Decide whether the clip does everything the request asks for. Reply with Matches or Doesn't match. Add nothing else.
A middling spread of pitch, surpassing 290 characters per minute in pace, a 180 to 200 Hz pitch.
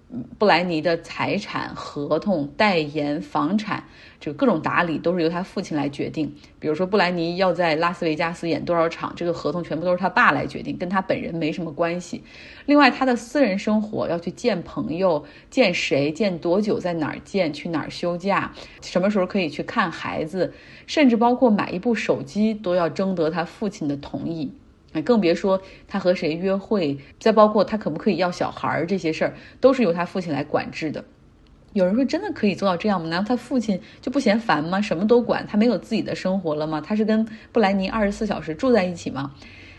Matches